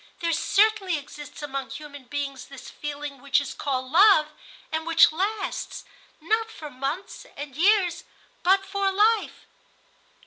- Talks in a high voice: Yes, very high, 315 Hz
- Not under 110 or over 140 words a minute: Yes, slow, 135 wpm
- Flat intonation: No, wide, 5.5 semitones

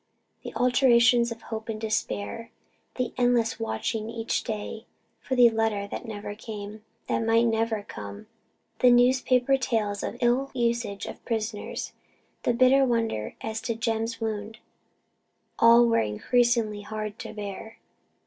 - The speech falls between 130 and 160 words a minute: Yes, average, 140 wpm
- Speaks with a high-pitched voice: Yes, high, 225 Hz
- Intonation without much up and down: Yes, narrow, 2.1 semitones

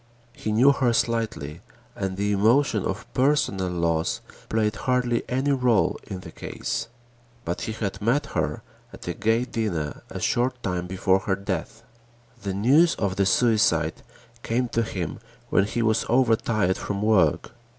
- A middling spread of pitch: Yes, average, 4.1 semitones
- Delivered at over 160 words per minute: No, average, 155 wpm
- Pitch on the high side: No, low, 110 Hz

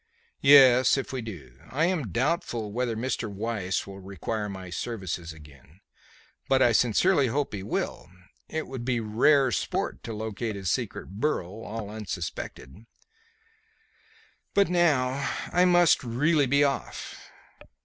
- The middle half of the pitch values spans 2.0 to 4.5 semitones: No, wide, 5.6 semitones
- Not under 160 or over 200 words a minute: No, slow, 135 wpm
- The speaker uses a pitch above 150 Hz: No, low, 115 Hz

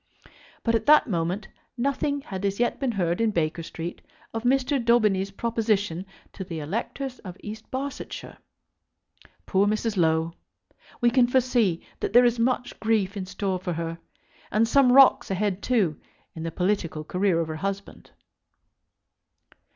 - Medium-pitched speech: No, high, 205 Hz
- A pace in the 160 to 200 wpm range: No, average, 150 wpm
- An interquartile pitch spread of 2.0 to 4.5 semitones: No, average, 5.1 semitones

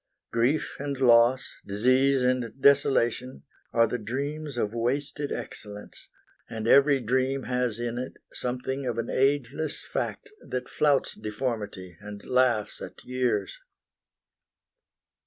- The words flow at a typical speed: No, slow, 120 wpm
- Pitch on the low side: Yes, low, 125 Hz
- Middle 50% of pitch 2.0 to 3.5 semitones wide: Yes, average, 2.8 semitones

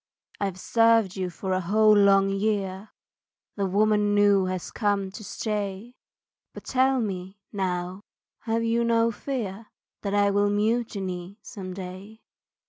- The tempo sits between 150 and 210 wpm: No, slow, 135 wpm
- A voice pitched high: Yes, high, 205 Hz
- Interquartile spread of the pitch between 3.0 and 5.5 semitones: No, narrow, 2.4 semitones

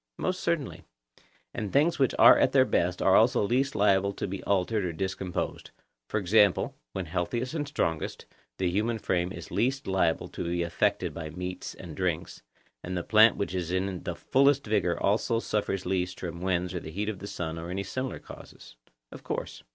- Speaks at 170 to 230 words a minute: Yes, average, 190 wpm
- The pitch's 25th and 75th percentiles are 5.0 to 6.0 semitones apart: No, average, 4.0 semitones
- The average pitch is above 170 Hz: No, very low, 95 Hz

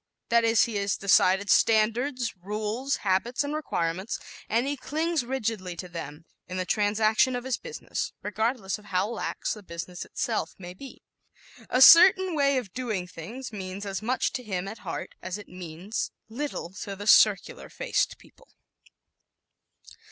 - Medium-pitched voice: No, high, 215 Hz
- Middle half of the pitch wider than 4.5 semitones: Yes, average, 5.2 semitones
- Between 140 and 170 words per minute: Yes, average, 160 wpm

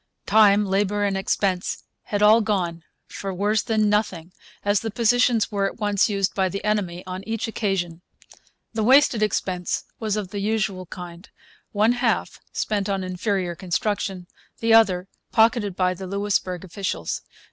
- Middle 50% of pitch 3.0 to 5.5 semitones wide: No, narrow, 2.6 semitones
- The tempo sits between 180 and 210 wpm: No, average, 155 wpm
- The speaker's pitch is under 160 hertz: No, high, 200 Hz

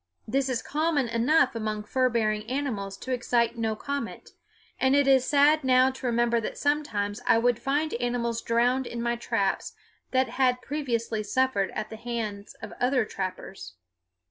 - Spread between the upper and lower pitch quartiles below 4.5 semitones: Yes, average, 2.7 semitones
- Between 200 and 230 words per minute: No, average, 165 wpm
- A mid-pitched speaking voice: No, high, 240 Hz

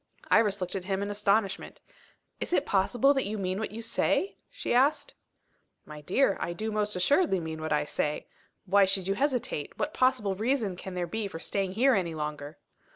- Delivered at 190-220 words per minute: Yes, average, 195 wpm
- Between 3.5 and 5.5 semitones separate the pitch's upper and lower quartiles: Yes, average, 4.0 semitones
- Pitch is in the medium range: No, high, 200 Hz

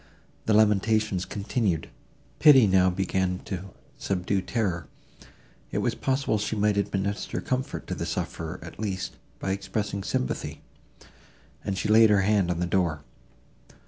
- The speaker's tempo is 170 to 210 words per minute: No, average, 140 wpm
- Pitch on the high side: No, low, 100 Hz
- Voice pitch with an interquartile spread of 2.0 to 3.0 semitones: Yes, narrow, 2.5 semitones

